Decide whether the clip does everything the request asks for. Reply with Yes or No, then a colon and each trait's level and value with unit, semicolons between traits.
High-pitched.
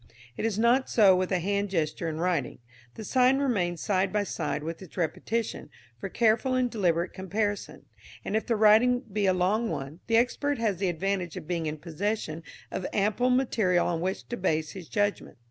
Yes: high, 195 Hz